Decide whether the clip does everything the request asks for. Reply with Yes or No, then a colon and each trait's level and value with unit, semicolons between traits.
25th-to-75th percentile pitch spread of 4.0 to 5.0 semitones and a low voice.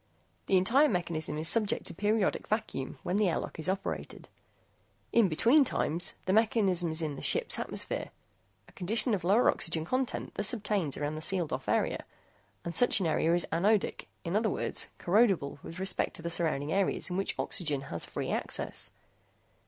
No: average, 4.7 semitones; medium, 185 Hz